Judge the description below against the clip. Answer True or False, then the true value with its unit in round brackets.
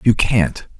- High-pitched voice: False (105 Hz)